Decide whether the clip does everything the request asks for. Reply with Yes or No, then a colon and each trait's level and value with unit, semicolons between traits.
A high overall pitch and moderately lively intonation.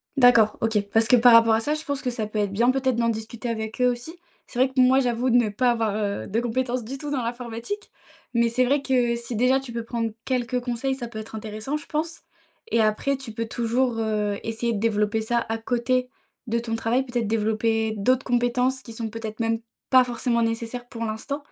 No: high, 235 Hz; narrow, 2.2 semitones